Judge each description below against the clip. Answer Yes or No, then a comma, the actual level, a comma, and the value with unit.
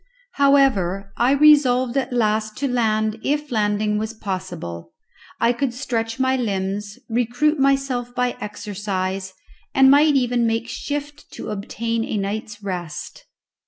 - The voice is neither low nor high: No, high, 230 Hz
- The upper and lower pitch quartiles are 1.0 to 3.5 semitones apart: No, average, 4.2 semitones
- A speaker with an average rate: No, slow, 130 wpm